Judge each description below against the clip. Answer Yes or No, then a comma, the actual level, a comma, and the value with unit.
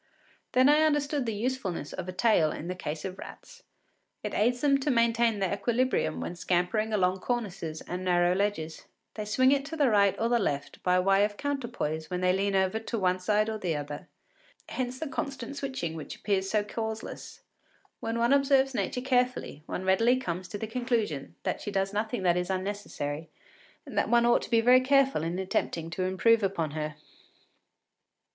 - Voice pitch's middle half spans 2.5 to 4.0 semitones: No, average, 5.2 semitones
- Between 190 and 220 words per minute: Yes, average, 195 wpm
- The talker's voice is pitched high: Yes, high, 205 Hz